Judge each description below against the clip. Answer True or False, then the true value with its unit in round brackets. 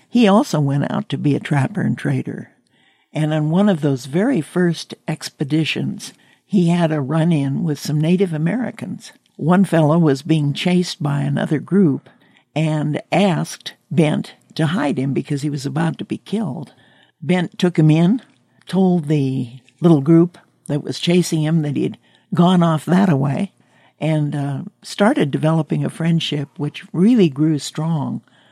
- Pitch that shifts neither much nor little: True (3.6 semitones)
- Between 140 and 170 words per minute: True (160 wpm)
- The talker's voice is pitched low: False (160 Hz)